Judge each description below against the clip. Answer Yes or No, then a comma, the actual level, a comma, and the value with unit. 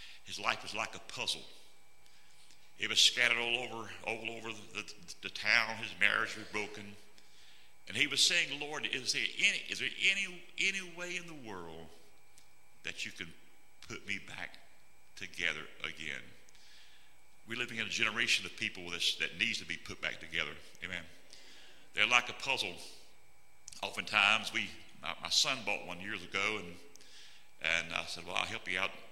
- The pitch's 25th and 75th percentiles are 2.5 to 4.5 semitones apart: Yes, average, 2.9 semitones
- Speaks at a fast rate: No, average, 170 wpm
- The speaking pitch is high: No, low, 110 Hz